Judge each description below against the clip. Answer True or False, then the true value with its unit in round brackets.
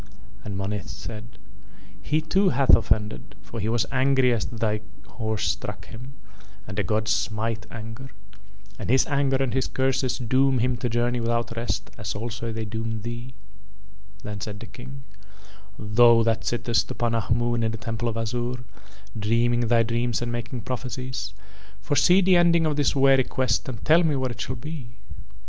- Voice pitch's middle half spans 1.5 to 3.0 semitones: True (2.6 semitones)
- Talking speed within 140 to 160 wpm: False (170 wpm)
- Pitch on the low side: True (120 Hz)